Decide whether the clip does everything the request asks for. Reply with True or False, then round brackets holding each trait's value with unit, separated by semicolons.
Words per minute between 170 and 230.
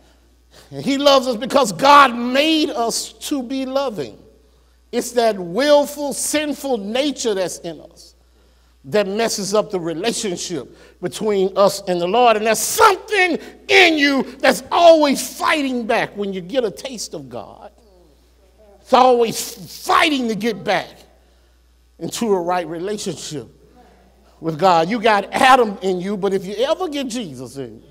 False (150 wpm)